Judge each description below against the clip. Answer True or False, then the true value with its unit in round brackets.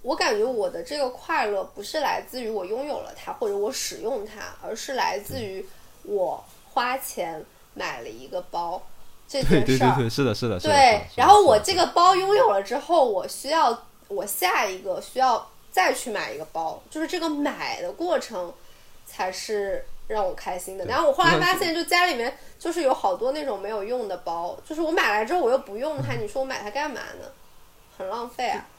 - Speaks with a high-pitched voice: True (270 Hz)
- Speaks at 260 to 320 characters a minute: True (290 characters per minute)